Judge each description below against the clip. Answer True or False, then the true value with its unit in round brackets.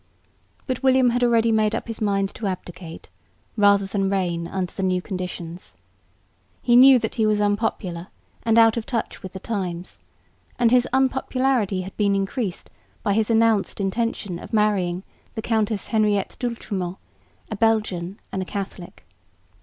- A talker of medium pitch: False (205 Hz)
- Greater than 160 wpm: False (155 wpm)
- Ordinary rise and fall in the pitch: True (3.3 semitones)